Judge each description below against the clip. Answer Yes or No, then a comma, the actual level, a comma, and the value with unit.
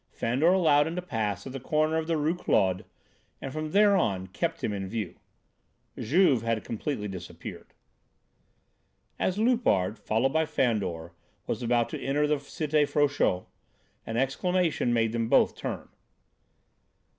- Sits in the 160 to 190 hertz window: No, low, 135 Hz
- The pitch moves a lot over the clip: Yes, wide, 6.1 semitones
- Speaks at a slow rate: No, average, 145 wpm